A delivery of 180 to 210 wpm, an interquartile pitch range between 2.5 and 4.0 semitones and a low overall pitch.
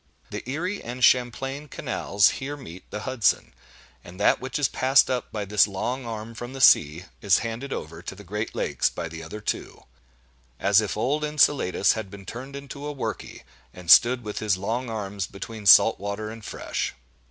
No: average, 185 wpm; average, 4.9 semitones; low, 110 Hz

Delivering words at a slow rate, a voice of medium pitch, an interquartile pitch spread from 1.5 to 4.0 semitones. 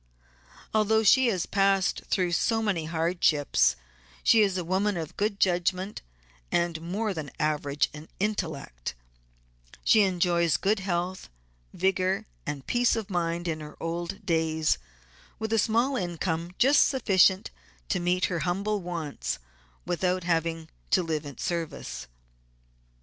Yes: slow, 130 wpm; medium, 180 Hz; average, 3.4 semitones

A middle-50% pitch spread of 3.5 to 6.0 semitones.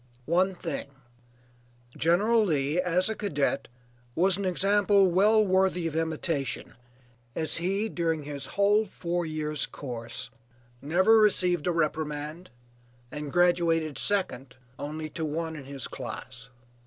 Yes: average, 4.0 semitones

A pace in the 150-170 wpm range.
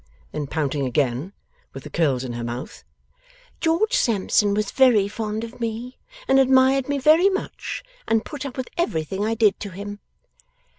Yes: average, 165 wpm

